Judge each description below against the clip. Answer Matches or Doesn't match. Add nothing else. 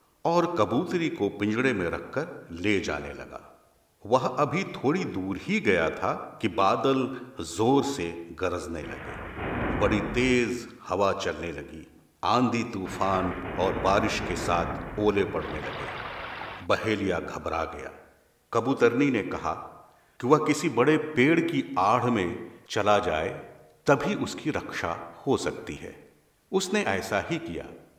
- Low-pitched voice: Matches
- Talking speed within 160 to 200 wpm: Doesn't match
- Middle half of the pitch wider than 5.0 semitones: Matches